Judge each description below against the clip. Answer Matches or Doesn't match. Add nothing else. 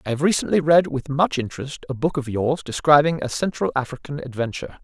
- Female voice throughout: Doesn't match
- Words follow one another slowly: Doesn't match